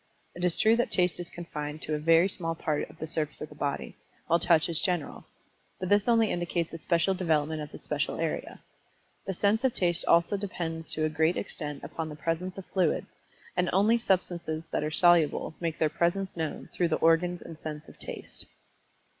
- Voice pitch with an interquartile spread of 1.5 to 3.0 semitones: Yes, narrow, 2.5 semitones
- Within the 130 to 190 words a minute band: No, fast, 205 wpm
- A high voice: No, medium, 170 Hz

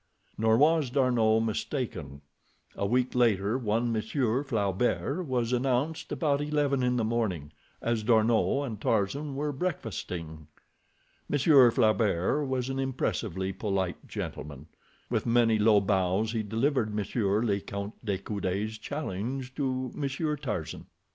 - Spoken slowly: Yes, slow, 130 wpm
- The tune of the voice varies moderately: Yes, average, 4.7 semitones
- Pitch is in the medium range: No, low, 115 Hz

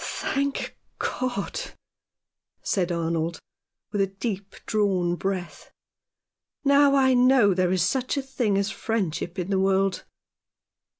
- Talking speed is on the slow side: Yes, slow, 125 wpm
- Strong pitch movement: Yes, wide, 5.7 semitones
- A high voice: Yes, high, 200 Hz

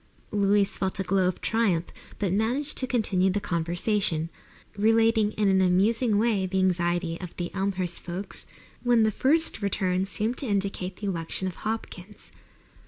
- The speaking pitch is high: Yes, high, 195 Hz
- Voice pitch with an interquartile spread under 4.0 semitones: Yes, average, 3.2 semitones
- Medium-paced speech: Yes, average, 160 wpm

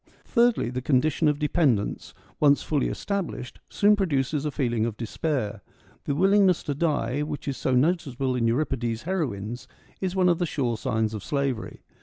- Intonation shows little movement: No, average, 5.3 semitones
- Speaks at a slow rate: No, average, 165 wpm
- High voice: No, medium, 140 Hz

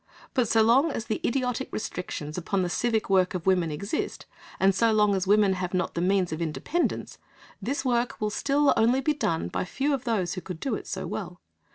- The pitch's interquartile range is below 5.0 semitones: No, average, 5.3 semitones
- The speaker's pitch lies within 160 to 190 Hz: No, high, 210 Hz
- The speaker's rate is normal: No, fast, 215 wpm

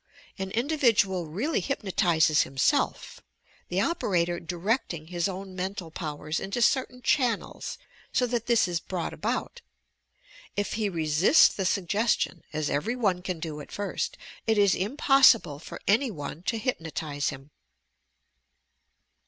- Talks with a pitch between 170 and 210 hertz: Yes, high, 190 Hz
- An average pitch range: No, wide, 5.8 semitones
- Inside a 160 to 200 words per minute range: No, slow, 135 wpm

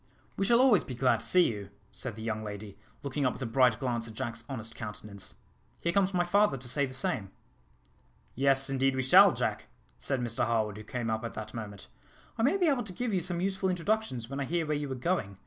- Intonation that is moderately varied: No, wide, 7.5 semitones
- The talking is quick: Yes, fast, 235 wpm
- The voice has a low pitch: Yes, low, 130 Hz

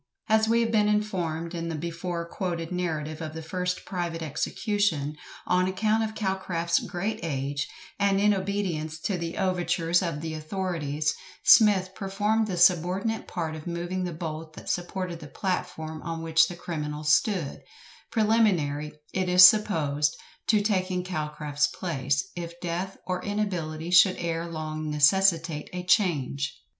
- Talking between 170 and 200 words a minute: No, average, 150 wpm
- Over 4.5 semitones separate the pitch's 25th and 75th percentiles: No, average, 3.4 semitones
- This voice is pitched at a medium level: Yes, medium, 175 Hz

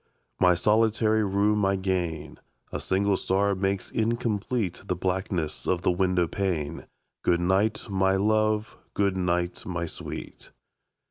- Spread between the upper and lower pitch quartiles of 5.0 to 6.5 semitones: No, average, 2.8 semitones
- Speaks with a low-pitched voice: Yes, very low, 95 Hz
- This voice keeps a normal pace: No, slow, 130 wpm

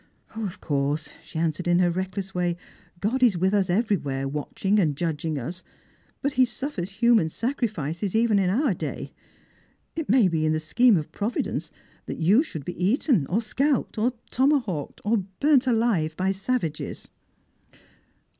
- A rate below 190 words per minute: Yes, average, 165 wpm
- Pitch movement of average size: No, wide, 6.3 semitones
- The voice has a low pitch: No, high, 190 Hz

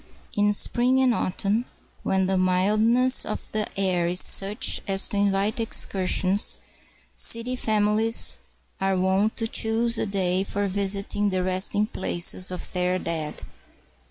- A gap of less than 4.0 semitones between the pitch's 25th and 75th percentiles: Yes, average, 2.7 semitones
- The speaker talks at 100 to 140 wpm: Yes, slow, 135 wpm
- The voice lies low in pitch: No, high, 200 Hz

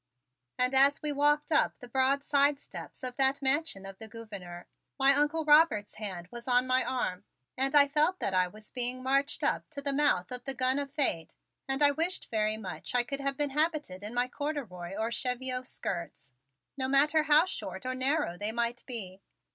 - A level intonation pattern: No, average, 4.5 semitones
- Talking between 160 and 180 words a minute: No, average, 200 wpm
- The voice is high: Yes, very high, 260 Hz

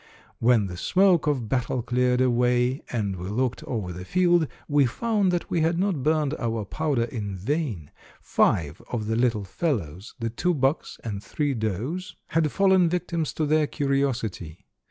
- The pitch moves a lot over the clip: Yes, wide, 6.2 semitones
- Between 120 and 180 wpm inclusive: Yes, average, 165 wpm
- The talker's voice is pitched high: No, low, 125 Hz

